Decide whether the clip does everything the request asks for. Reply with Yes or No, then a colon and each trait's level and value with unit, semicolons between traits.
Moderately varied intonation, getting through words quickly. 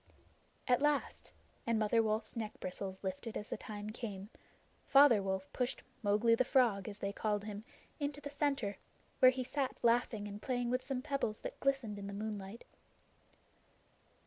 No: average, 3.8 semitones; average, 165 wpm